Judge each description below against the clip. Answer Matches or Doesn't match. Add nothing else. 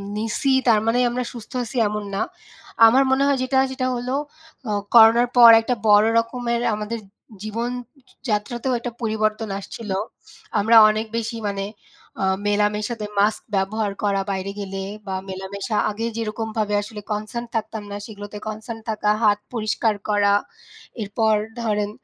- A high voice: Matches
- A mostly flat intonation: Matches